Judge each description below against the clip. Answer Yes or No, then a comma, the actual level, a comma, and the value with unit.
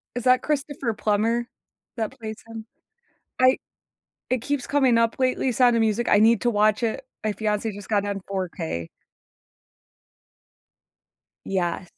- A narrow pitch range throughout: No, average, 3.2 semitones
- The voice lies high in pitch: Yes, high, 225 Hz